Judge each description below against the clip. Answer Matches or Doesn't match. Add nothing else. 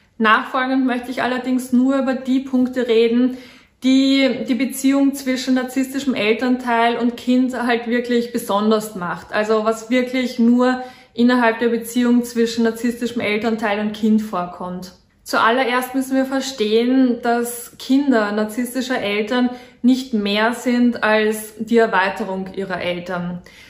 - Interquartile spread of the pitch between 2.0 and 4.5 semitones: Matches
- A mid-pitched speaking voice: Doesn't match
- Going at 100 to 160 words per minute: Matches